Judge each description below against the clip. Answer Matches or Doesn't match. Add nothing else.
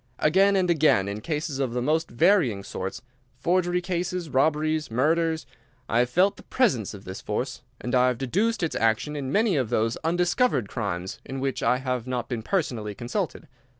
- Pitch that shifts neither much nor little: Doesn't match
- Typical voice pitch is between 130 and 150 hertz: Matches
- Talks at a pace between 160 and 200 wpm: Matches